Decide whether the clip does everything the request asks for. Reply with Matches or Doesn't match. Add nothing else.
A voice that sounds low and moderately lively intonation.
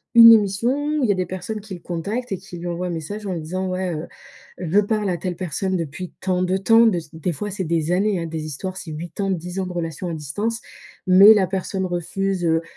Doesn't match